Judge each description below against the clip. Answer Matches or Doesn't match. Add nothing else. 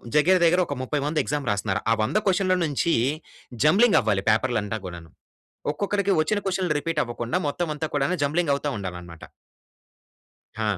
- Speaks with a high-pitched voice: Doesn't match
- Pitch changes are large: Matches